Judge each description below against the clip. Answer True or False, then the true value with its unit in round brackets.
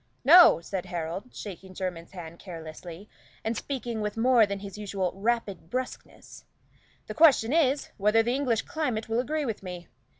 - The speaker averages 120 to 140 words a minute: False (155 wpm)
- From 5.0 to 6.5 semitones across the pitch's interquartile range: True (5.3 semitones)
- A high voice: True (210 Hz)